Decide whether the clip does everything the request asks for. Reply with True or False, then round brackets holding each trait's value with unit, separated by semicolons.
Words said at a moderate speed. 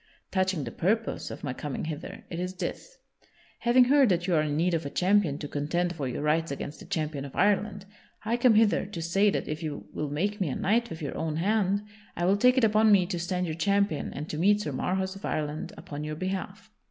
False (240 wpm)